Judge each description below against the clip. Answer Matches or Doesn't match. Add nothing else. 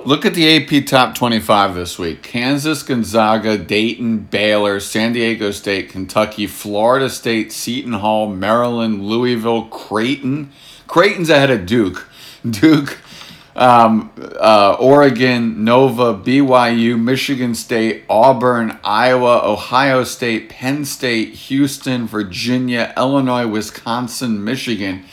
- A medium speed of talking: Doesn't match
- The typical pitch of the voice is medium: Doesn't match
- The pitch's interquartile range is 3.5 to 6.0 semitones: Doesn't match